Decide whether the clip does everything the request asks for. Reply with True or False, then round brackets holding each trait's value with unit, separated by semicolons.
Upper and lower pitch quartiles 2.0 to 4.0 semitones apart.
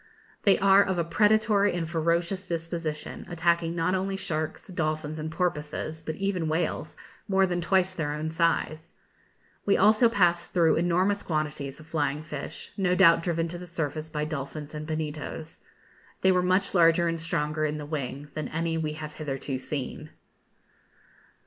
True (2.8 semitones)